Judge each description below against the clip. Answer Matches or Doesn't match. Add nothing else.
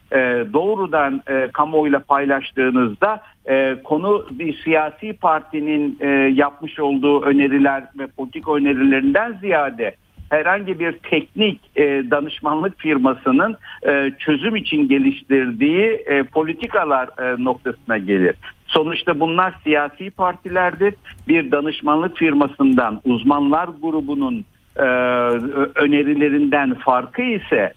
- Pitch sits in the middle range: Matches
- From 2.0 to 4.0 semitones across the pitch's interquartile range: Doesn't match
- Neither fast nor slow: Doesn't match